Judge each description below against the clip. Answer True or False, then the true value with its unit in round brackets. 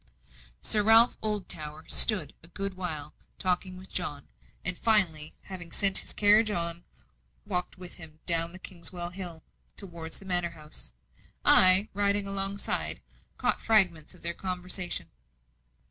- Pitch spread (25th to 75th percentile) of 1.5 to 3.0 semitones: True (2.7 semitones)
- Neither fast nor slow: False (130 wpm)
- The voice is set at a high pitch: False (180 Hz)